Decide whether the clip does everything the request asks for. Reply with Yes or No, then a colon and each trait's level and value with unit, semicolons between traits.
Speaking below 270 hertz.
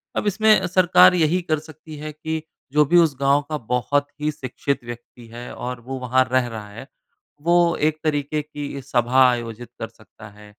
Yes: medium, 140 Hz